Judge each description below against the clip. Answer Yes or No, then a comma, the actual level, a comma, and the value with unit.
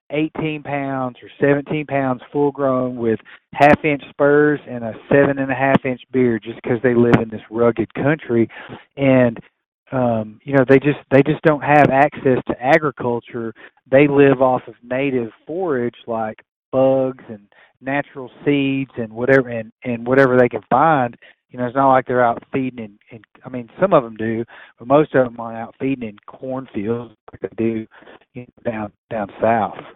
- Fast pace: No, average, 170 wpm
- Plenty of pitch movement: No, average, 2.9 semitones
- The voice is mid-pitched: No, low, 130 Hz